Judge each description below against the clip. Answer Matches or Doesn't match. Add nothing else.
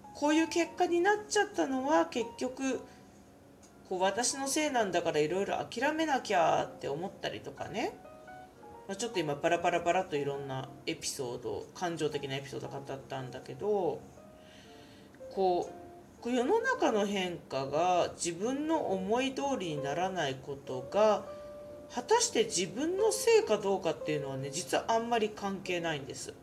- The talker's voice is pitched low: Doesn't match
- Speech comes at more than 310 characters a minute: Matches